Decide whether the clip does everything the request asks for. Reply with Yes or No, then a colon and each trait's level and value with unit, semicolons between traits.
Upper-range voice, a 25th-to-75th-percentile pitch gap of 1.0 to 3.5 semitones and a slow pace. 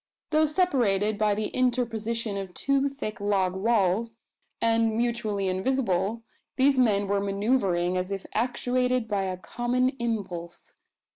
No: high, 220 Hz; average, 4.0 semitones; slow, 130 wpm